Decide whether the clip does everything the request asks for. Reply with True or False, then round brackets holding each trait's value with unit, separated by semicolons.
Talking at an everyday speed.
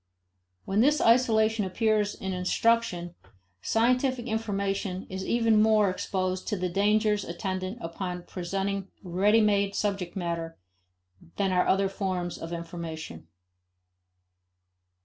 False (110 wpm)